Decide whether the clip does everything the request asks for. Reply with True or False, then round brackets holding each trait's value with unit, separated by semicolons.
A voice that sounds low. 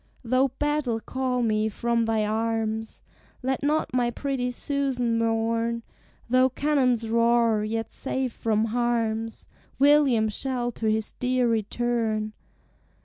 False (235 Hz)